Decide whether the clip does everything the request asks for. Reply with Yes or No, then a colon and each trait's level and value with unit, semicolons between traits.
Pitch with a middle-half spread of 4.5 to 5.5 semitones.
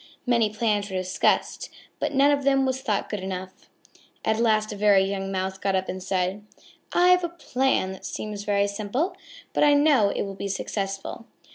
Yes: average, 5.2 semitones